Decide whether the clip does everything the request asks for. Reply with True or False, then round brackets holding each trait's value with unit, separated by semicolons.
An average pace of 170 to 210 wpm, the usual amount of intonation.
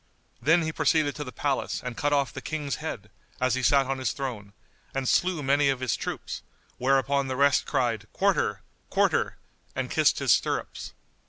False (180 wpm; 2.2 semitones)